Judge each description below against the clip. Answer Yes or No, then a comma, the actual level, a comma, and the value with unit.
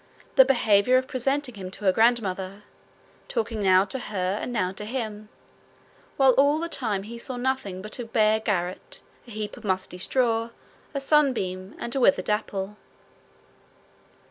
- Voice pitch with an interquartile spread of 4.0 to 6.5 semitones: Yes, average, 4.6 semitones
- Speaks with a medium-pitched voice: No, high, 220 Hz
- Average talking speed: Yes, average, 160 wpm